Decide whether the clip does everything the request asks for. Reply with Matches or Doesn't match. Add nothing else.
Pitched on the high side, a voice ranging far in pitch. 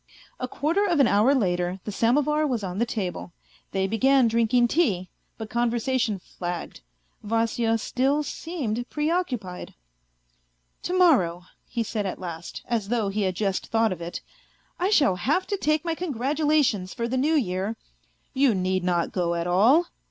Matches